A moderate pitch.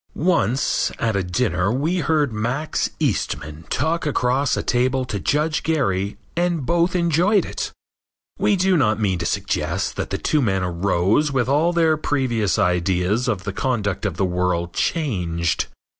No: low, 125 Hz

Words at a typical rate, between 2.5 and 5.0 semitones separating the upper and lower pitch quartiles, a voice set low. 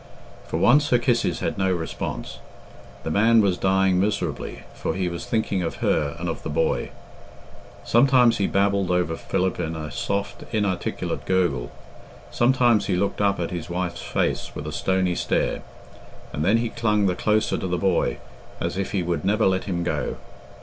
Yes: average, 175 wpm; average, 3.3 semitones; very low, 95 Hz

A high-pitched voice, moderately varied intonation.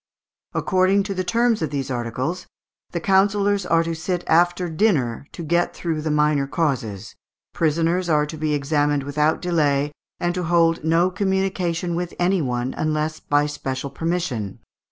No: medium, 165 Hz; average, 3.5 semitones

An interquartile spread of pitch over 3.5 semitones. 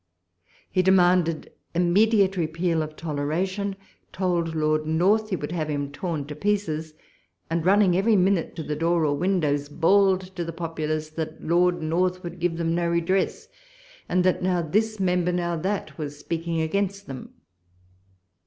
No: average, 3.0 semitones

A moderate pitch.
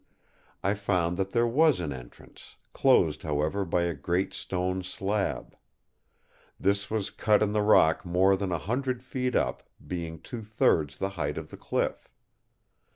No: very low, 95 Hz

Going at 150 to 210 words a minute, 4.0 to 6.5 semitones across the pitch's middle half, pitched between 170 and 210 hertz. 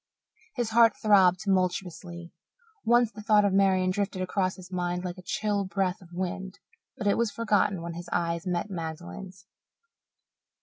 No: average, 160 wpm; narrow, 2.4 semitones; medium, 185 Hz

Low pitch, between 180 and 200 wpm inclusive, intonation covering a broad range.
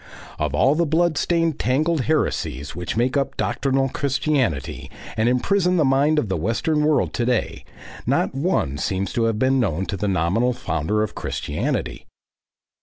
No: low, 130 Hz; average, 165 wpm; wide, 6.4 semitones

